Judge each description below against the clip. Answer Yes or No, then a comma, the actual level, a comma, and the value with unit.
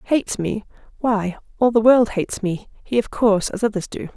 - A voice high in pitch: Yes, high, 215 Hz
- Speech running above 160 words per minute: Yes, average, 200 wpm